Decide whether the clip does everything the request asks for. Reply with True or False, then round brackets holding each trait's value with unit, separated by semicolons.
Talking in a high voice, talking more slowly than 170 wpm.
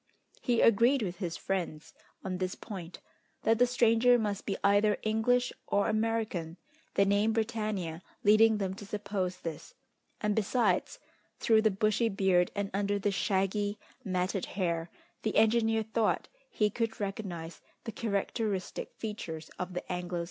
True (205 Hz; 150 wpm)